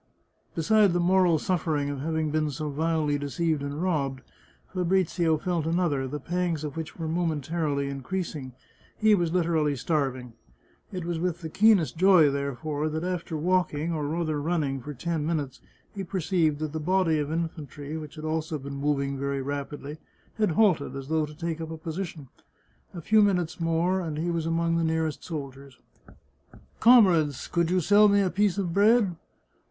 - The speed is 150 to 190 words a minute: Yes, average, 180 wpm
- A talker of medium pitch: Yes, medium, 160 Hz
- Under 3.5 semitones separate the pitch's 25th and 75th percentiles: Yes, average, 3.1 semitones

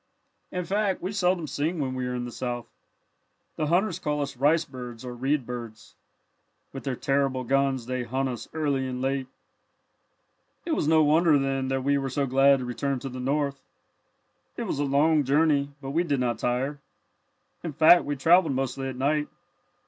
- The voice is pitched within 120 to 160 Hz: Yes, medium, 140 Hz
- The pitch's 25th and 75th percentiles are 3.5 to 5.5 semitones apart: No, average, 2.8 semitones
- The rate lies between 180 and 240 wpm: Yes, average, 185 wpm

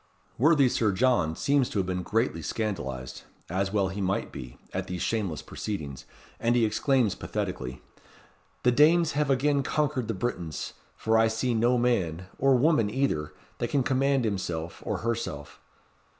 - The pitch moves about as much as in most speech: No, wide, 6.0 semitones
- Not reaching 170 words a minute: Yes, average, 160 wpm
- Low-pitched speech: Yes, low, 110 Hz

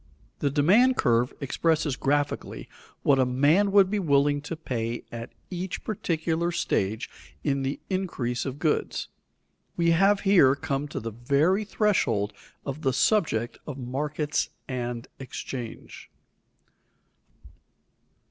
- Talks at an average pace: No, slow, 120 wpm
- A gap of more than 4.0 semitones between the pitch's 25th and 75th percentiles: Yes, average, 5.2 semitones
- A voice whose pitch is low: No, medium, 145 Hz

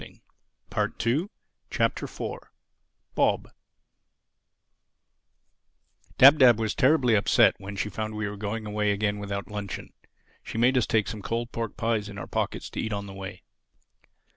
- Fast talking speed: No, average, 150 wpm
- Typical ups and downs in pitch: No, narrow, 2.3 semitones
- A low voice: Yes, low, 105 Hz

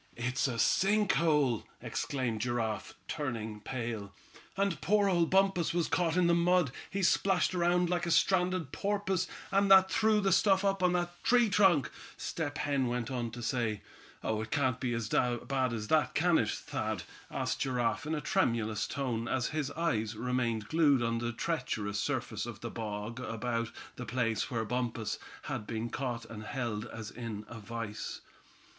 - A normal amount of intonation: No, wide, 7.2 semitones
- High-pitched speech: No, low, 130 Hz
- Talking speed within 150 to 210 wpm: Yes, average, 175 wpm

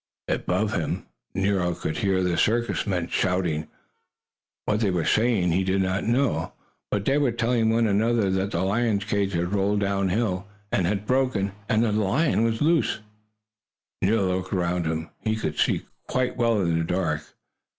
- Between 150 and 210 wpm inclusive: Yes, average, 170 wpm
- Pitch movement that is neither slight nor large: Yes, average, 3.7 semitones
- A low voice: Yes, low, 100 Hz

